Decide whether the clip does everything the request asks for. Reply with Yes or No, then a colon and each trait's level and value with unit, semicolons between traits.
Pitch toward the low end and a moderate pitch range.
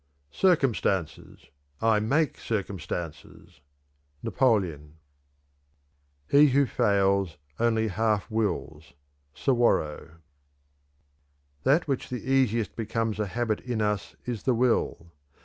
Yes: low, 110 Hz; average, 4.6 semitones